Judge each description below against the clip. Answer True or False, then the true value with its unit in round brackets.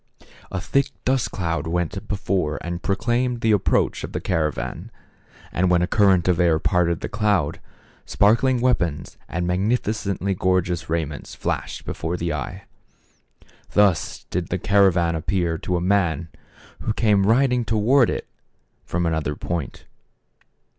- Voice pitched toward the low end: True (90 Hz)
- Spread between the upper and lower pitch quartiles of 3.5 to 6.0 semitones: True (3.8 semitones)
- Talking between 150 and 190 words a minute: False (140 wpm)